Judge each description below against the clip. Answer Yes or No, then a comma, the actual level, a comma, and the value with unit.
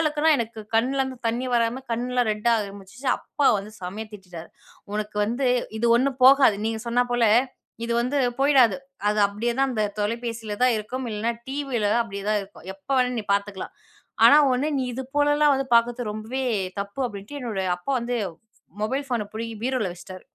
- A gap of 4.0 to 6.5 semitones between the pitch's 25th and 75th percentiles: No, average, 3.6 semitones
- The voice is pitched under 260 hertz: Yes, high, 235 Hz